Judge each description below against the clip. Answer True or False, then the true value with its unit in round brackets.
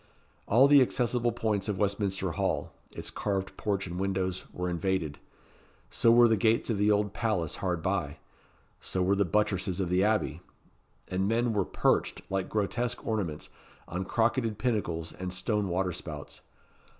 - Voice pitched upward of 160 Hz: False (100 Hz)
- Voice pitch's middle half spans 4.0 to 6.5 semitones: False (3.2 semitones)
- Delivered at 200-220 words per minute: False (160 wpm)